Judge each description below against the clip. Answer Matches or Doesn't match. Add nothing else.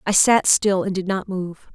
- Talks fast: Matches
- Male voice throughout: Doesn't match